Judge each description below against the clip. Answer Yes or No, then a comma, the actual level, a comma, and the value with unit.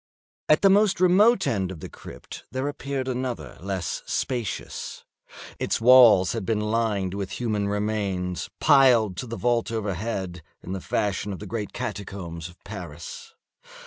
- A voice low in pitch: Yes, low, 105 Hz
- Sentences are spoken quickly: No, average, 150 wpm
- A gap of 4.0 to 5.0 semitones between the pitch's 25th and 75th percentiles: Yes, average, 4.7 semitones